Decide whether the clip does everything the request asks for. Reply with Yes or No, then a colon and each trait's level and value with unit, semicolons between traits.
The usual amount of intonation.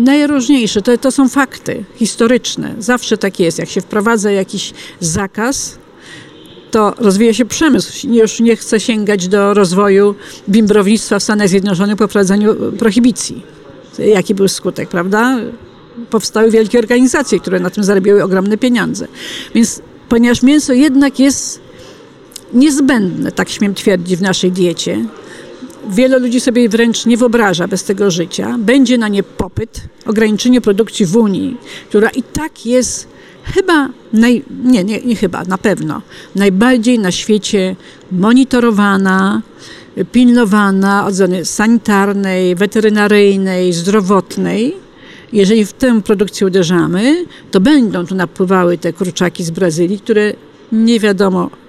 Yes: average, 3.6 semitones